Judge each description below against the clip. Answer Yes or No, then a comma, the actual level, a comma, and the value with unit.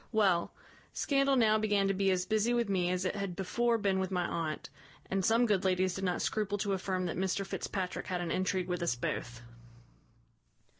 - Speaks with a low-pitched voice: No, high, 190 Hz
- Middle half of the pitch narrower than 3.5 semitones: Yes, narrow, 2.5 semitones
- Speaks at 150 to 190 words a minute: No, average, 200 wpm